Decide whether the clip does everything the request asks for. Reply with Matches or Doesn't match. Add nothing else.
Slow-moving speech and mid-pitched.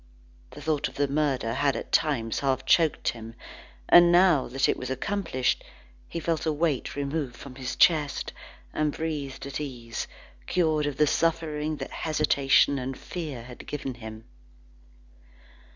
Doesn't match